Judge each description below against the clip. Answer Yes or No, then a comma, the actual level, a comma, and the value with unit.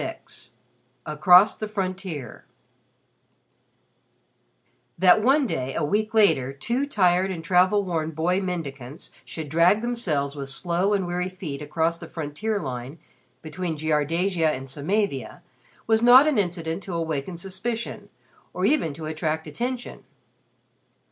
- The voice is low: No, medium, 175 Hz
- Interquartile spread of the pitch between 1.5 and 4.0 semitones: No, average, 4.9 semitones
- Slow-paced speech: Yes, slow, 130 wpm